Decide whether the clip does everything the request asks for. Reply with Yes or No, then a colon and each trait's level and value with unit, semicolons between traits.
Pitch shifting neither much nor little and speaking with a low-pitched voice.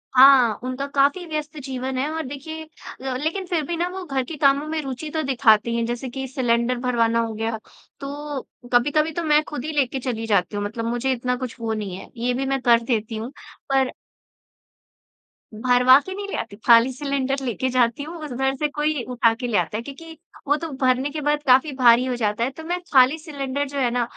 No: average, 3.5 semitones; very high, 260 Hz